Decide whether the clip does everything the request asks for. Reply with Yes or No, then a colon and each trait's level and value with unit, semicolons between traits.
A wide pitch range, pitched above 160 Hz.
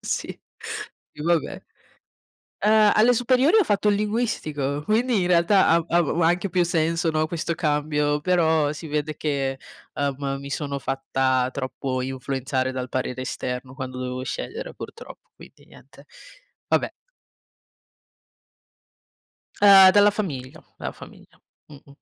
No: wide, 6.0 semitones; medium, 155 Hz